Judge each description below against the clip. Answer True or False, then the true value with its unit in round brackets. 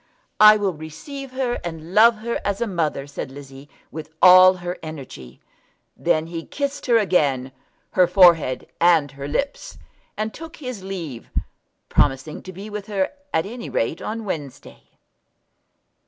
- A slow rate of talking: False (150 wpm)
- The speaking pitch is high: False (180 Hz)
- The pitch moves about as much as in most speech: False (6.0 semitones)